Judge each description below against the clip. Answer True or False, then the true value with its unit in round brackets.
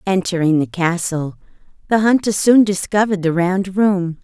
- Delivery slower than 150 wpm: True (140 wpm)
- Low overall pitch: False (185 Hz)